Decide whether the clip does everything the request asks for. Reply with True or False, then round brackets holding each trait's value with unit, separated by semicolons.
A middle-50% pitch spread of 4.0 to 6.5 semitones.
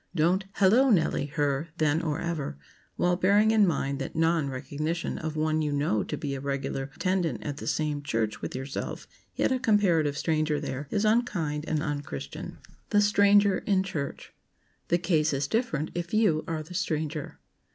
True (4.5 semitones)